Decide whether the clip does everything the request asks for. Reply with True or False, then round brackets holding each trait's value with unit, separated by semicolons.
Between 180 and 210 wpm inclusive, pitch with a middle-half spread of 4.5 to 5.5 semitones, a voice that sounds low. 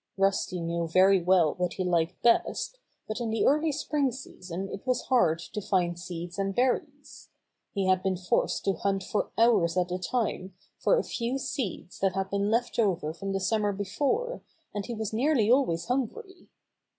False (185 wpm; 5.1 semitones; 195 Hz)